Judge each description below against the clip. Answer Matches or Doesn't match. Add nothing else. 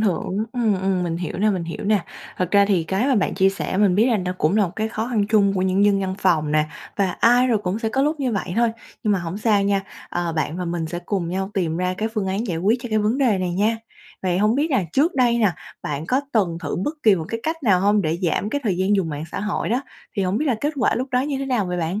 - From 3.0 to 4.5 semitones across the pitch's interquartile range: Matches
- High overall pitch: Matches